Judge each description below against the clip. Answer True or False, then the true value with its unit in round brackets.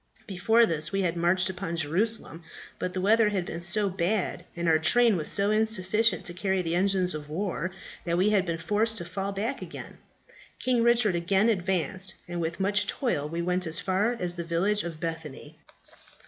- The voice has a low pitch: False (185 Hz)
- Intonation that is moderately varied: True (3.5 semitones)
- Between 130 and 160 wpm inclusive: False (190 wpm)